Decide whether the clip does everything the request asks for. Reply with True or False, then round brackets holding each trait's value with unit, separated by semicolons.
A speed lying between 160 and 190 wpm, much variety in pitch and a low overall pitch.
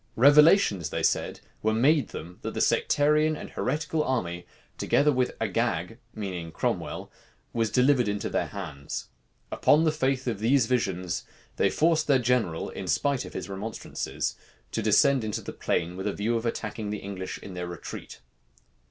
True (165 wpm; 6.3 semitones; 115 Hz)